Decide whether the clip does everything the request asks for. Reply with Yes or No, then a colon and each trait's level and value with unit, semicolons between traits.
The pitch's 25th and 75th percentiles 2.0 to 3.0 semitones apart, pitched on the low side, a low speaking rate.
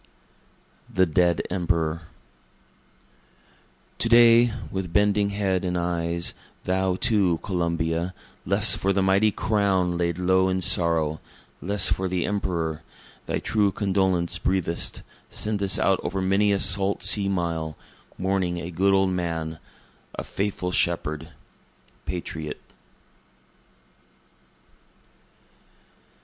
Yes: narrow, 2.5 semitones; very low, 95 Hz; slow, 110 wpm